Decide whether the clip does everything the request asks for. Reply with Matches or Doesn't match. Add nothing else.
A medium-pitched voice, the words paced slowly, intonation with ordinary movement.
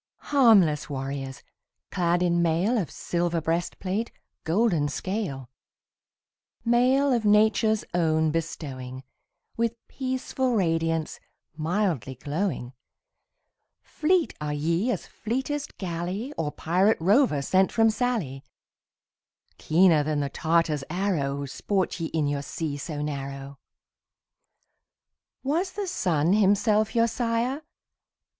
Doesn't match